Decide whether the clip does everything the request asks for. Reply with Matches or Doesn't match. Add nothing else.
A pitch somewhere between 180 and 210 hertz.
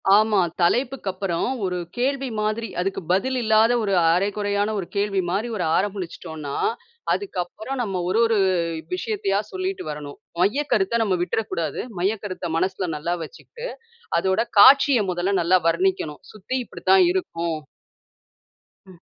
Matches